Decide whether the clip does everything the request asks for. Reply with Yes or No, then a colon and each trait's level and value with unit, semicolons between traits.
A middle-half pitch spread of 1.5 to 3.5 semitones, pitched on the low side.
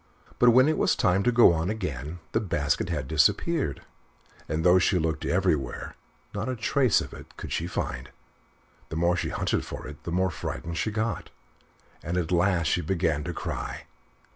No: average, 4.1 semitones; very low, 90 Hz